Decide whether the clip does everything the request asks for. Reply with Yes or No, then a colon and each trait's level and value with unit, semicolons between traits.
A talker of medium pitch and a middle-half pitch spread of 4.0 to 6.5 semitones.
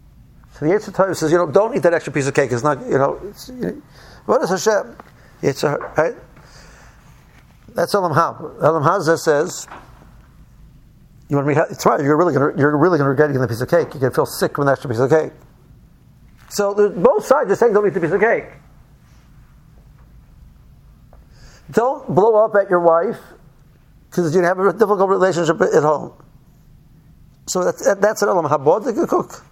Yes: medium, 165 Hz; average, 5.1 semitones